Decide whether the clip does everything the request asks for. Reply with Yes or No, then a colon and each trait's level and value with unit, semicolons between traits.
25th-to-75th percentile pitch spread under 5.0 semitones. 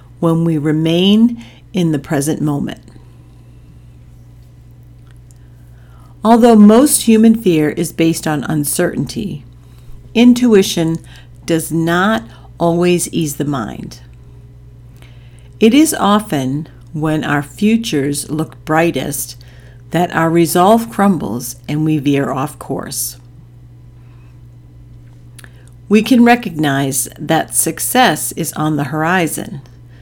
No: wide, 5.5 semitones